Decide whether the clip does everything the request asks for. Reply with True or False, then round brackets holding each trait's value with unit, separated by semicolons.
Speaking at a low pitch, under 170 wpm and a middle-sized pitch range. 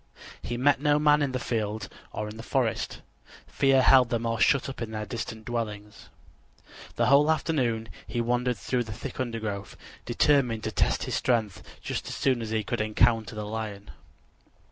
False (115 Hz; 180 wpm; 3.1 semitones)